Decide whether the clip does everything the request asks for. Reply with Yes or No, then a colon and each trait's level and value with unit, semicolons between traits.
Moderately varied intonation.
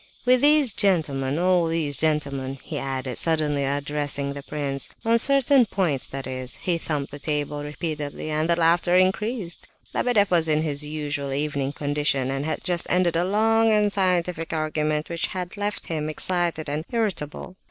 Yes: average, 4.2 semitones